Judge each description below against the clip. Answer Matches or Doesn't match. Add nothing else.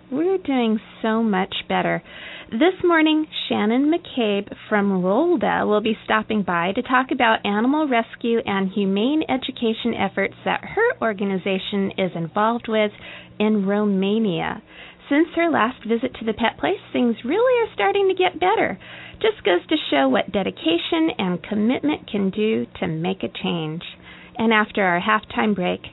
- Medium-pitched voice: Doesn't match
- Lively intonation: Matches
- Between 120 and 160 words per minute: Matches